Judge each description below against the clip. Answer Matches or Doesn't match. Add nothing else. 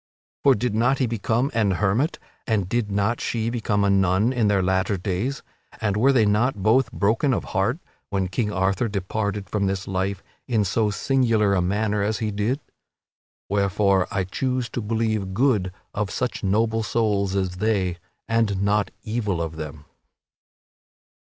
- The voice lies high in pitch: Doesn't match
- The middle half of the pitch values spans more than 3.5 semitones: Doesn't match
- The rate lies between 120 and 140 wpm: Doesn't match